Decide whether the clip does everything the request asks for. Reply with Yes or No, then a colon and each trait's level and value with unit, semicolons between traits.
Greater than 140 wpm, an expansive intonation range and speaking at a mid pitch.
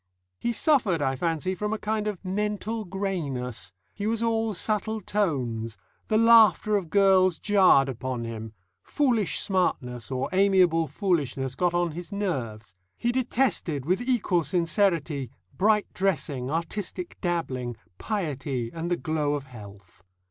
No: slow, 135 wpm; wide, 7.4 semitones; medium, 175 Hz